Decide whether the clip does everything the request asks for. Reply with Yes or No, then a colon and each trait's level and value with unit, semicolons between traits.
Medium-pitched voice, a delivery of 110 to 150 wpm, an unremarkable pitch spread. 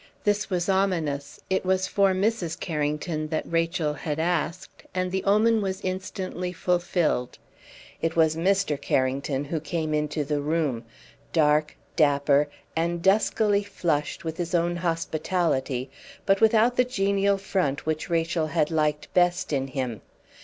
Yes: medium, 165 Hz; average, 140 wpm; average, 3.9 semitones